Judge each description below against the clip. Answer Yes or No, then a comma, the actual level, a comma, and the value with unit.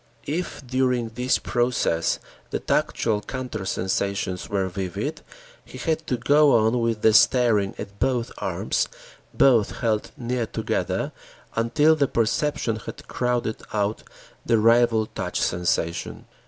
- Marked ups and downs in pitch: No, average, 3.2 semitones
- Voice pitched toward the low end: Yes, low, 115 Hz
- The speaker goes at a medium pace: No, slow, 125 wpm